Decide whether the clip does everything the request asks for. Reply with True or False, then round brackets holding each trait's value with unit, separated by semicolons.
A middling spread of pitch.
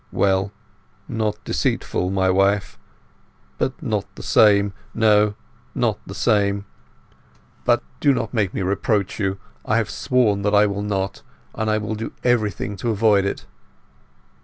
False (1.7 semitones)